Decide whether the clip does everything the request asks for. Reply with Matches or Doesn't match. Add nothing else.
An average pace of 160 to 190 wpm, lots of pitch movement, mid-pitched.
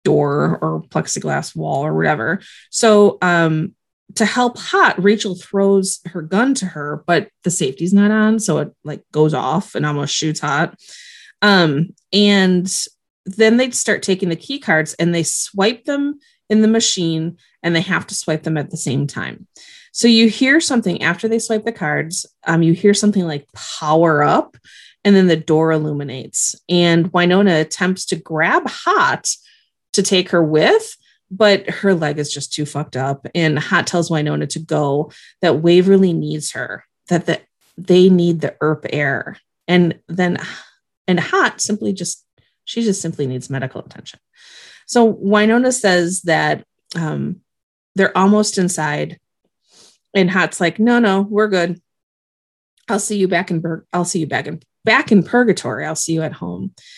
Doesn't match